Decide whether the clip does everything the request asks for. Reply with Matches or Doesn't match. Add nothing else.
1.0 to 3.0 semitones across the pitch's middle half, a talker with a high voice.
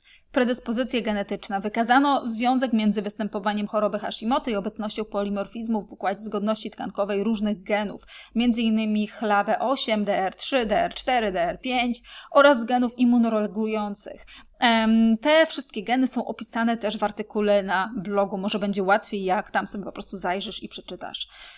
Matches